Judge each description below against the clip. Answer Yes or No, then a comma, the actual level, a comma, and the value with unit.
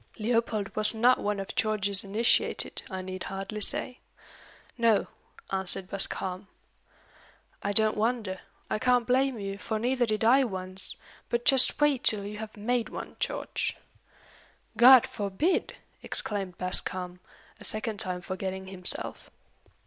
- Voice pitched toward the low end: No, high, 210 Hz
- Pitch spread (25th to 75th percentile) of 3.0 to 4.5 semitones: Yes, average, 3.6 semitones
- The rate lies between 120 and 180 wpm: Yes, slow, 135 wpm